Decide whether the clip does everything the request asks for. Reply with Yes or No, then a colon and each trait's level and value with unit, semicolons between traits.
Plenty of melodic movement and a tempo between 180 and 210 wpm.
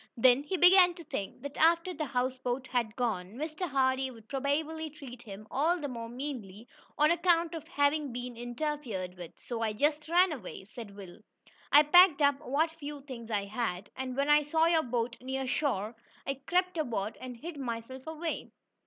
No: average, 4.8 semitones; average, 185 wpm